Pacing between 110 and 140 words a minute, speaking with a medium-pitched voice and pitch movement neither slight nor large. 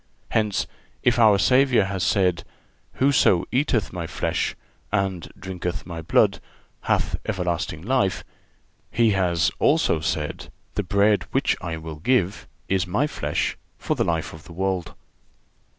No: slow, 135 wpm; very low, 95 Hz; average, 4.0 semitones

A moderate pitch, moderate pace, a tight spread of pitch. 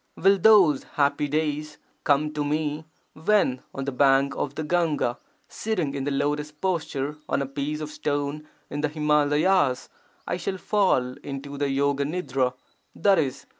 Yes: medium, 150 Hz; average, 155 wpm; narrow, 2.1 semitones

